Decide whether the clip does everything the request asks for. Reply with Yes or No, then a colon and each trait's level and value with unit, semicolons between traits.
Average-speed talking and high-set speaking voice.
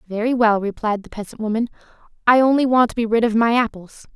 No: fast, 215 wpm; high, 225 Hz